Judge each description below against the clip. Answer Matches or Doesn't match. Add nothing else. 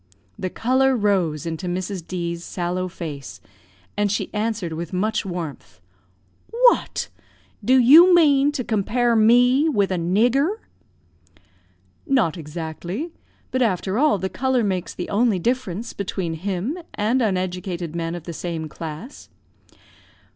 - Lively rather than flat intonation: Matches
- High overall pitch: Matches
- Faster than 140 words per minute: Doesn't match